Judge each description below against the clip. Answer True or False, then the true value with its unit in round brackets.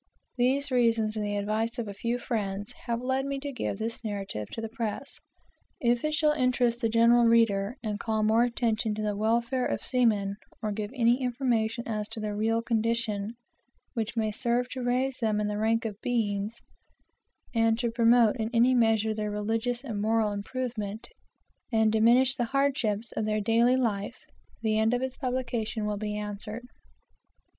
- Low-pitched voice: False (225 Hz)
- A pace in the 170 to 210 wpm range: True (180 wpm)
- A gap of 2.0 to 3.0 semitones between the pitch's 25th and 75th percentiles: True (2.4 semitones)